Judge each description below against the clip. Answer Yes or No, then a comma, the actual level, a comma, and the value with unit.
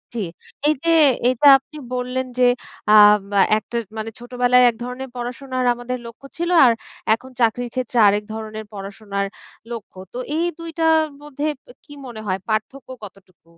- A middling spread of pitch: Yes, average, 3.2 semitones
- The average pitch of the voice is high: Yes, high, 245 Hz